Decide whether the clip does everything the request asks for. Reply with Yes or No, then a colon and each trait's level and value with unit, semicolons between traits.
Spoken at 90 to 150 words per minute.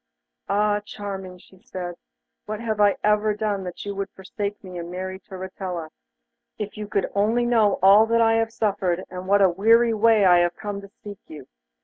No: average, 190 wpm